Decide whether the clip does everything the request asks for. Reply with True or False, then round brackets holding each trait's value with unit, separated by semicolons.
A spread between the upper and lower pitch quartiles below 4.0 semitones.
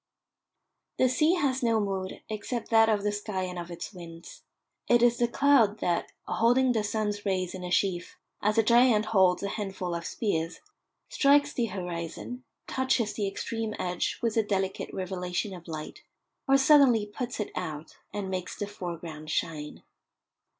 False (4.6 semitones)